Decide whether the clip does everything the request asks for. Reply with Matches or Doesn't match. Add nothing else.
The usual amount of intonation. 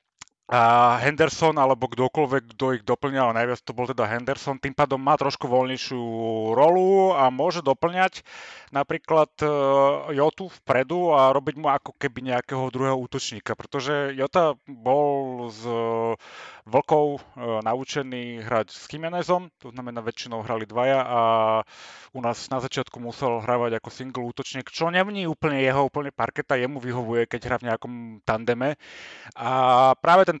Matches